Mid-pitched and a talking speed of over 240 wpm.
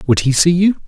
Yes: medium, 160 Hz; fast, 275 wpm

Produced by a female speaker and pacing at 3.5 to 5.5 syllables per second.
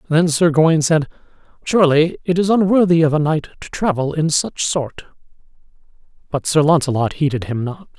No: male; 5.4 syllables/s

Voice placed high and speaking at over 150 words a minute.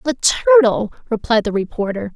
No: high, 215 Hz; average, 140 wpm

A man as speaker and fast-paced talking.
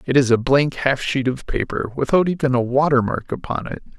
Yes: male; fast, 225 wpm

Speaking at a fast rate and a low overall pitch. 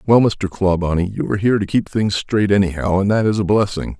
Yes: fast, 240 wpm; low, 100 Hz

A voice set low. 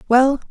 No: very high, 260 Hz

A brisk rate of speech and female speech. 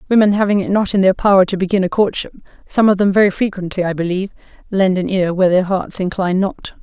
Yes: fast, 230 wpm; female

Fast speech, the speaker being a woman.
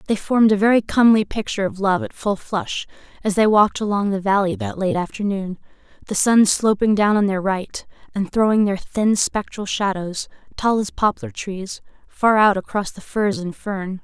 No: average, 190 wpm; female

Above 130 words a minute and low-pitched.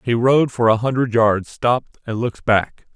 Yes: fast, 205 wpm; low, 115 Hz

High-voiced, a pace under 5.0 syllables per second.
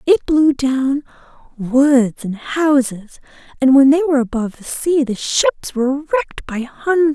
Yes: very high, 275 Hz; 4.3 syllables/s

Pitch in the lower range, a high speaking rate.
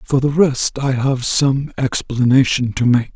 No: low, 130 Hz; average, 170 wpm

